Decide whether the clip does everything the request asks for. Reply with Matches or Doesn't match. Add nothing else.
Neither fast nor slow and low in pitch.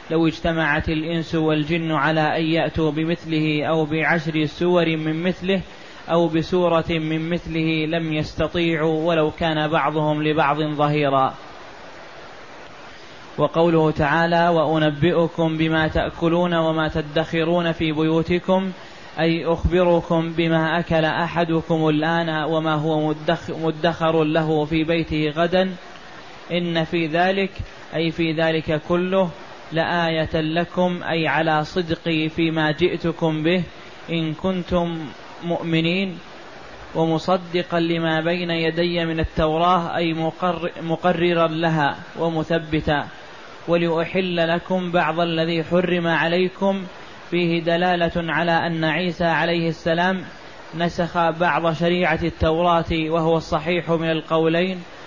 Doesn't match